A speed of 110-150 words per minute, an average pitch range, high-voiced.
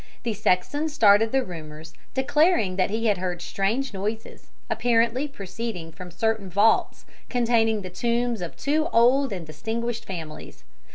Yes: average, 145 wpm; average, 4.6 semitones; high, 220 Hz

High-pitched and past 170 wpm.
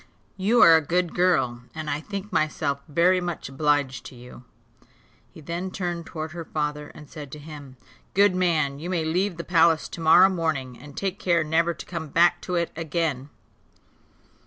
No: medium, 160 Hz; average, 180 wpm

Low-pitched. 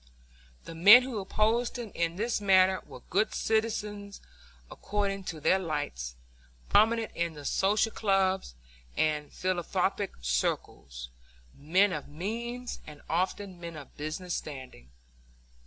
No: medium, 185 Hz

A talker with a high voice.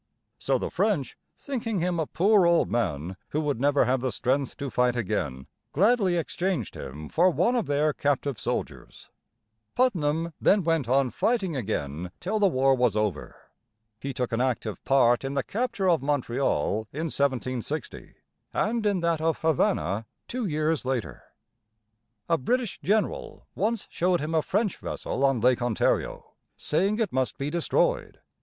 No: medium, 145 Hz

